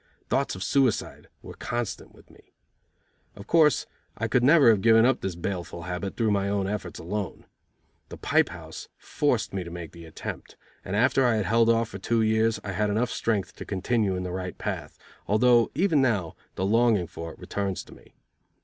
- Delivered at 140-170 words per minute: No, average, 195 wpm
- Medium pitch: No, low, 105 Hz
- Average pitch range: Yes, average, 3.8 semitones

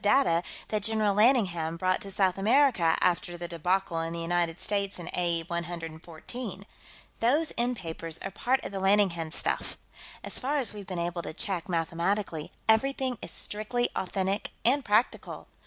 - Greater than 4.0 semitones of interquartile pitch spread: Yes, average, 4.5 semitones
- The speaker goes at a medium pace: Yes, average, 160 wpm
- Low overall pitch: No, high, 190 Hz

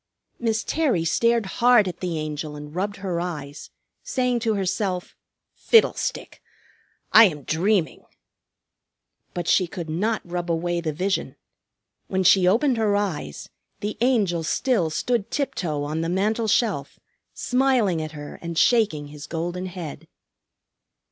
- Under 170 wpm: Yes, slow, 135 wpm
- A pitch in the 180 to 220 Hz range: Yes, medium, 185 Hz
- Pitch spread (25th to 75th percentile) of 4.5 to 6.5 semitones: Yes, average, 5.2 semitones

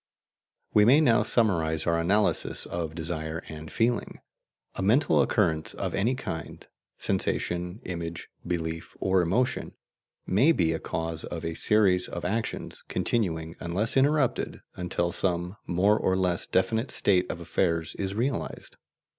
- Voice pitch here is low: Yes, very low, 90 Hz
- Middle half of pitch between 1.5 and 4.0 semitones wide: No, average, 4.4 semitones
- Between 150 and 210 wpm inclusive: No, average, 140 wpm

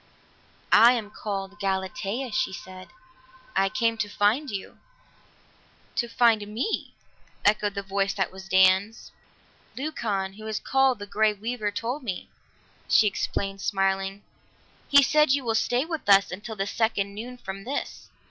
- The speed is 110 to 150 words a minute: Yes, average, 145 wpm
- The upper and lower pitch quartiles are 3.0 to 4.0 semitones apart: Yes, average, 3.4 semitones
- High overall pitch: Yes, high, 210 Hz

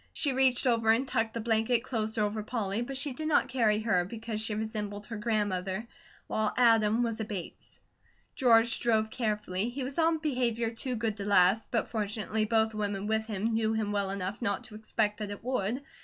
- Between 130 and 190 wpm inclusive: No, average, 200 wpm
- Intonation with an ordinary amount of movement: No, narrow, 2.1 semitones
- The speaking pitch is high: Yes, high, 220 Hz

